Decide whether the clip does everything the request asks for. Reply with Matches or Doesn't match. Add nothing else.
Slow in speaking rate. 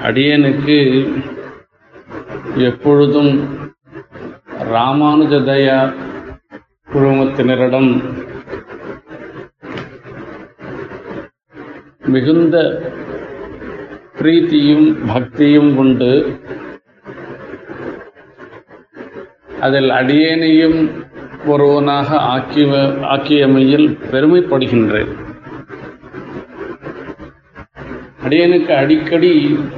Matches